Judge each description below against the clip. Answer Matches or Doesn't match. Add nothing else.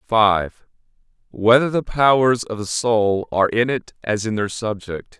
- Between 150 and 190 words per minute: Matches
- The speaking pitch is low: Matches